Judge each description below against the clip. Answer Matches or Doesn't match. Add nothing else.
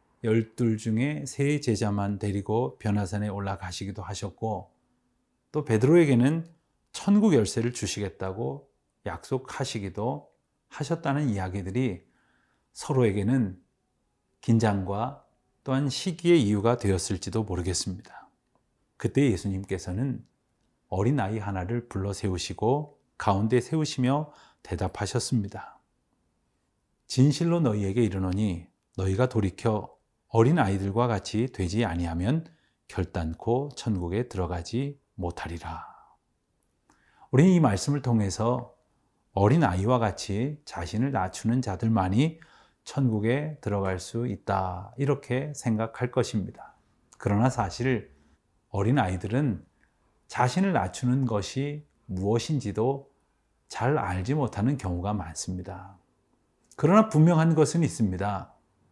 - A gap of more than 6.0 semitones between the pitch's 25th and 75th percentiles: Doesn't match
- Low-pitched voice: Matches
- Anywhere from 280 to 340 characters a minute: Doesn't match